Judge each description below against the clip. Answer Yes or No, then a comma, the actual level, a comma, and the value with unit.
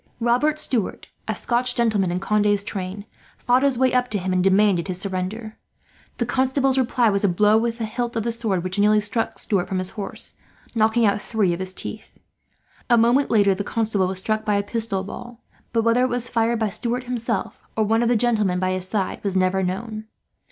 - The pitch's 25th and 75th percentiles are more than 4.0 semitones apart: No, average, 3.6 semitones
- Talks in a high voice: Yes, high, 215 Hz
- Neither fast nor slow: No, fast, 215 wpm